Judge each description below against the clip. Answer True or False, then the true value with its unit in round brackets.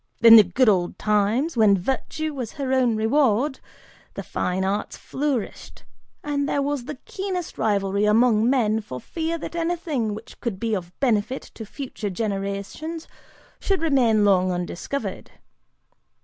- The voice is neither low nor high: False (230 Hz)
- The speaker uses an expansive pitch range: True (5.7 semitones)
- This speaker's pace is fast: False (145 wpm)